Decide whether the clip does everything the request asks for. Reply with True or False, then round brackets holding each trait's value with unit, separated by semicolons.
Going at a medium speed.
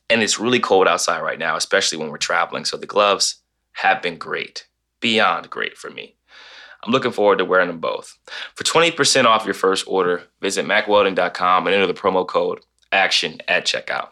True (185 wpm)